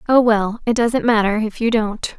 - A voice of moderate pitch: No, high, 225 Hz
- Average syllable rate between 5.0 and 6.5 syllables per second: No, 4.6 syllables/s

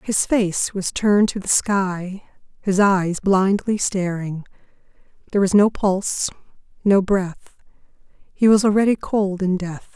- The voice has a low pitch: No, high, 195 Hz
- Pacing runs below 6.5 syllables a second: Yes, 4.1 syllables/s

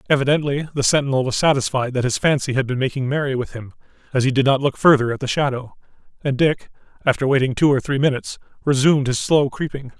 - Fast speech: Yes, fast, 210 wpm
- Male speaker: Yes, male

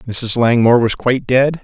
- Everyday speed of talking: Yes, average, 185 wpm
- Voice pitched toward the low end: Yes, low, 120 Hz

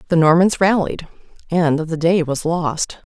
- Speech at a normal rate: Yes, average, 155 wpm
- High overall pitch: No, medium, 165 Hz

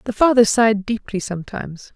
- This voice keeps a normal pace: Yes, average, 155 wpm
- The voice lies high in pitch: Yes, high, 210 Hz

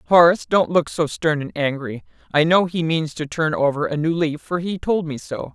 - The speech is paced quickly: Yes, fast, 240 wpm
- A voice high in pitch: No, medium, 160 Hz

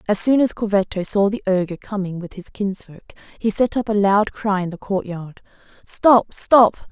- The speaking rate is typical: Yes, average, 190 wpm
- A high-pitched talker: Yes, high, 200 Hz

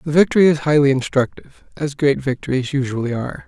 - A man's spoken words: Yes, male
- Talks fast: No, average, 175 wpm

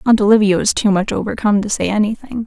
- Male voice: No, female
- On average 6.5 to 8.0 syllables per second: Yes, 6.8 syllables/s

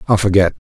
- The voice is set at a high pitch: No, very low, 95 Hz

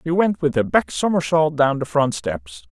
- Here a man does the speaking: Yes, male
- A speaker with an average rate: No, fast, 220 wpm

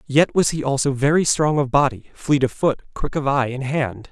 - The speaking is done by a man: Yes, male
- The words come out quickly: Yes, fast, 235 wpm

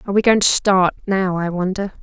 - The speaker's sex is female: Yes, female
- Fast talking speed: Yes, fast, 235 wpm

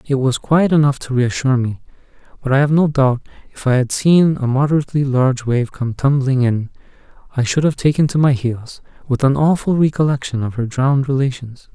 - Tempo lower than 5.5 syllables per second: No, 5.6 syllables/s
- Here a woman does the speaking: No, male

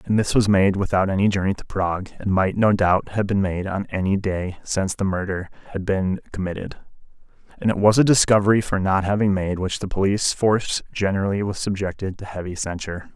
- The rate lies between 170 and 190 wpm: No, average, 200 wpm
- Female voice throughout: No, male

